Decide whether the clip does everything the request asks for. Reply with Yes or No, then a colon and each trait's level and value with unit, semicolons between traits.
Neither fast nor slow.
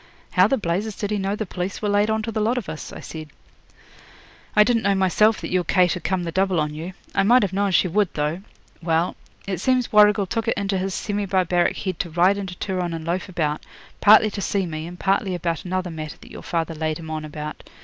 No: fast, 240 wpm